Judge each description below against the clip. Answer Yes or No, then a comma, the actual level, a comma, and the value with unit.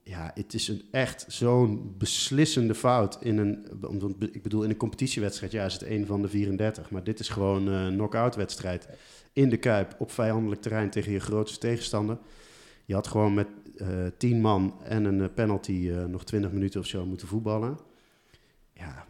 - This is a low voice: Yes, low, 105 Hz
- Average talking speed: Yes, average, 180 wpm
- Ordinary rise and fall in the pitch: No, narrow, 2.3 semitones